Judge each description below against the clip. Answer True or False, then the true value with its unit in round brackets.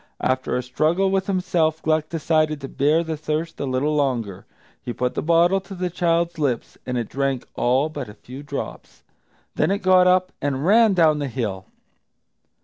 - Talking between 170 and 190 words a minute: True (185 wpm)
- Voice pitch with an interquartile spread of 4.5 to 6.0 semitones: True (4.8 semitones)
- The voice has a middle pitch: True (155 Hz)